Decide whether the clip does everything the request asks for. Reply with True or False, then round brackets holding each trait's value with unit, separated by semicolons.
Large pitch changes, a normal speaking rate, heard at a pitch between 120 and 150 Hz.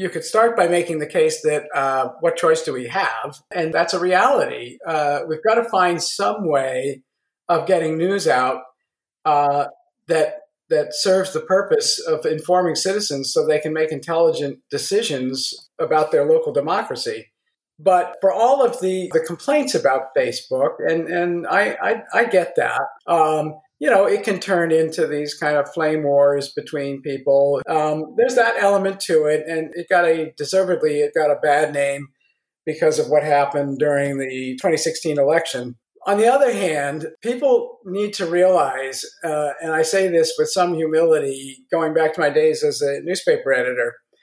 False (7.5 semitones; 170 wpm; 170 Hz)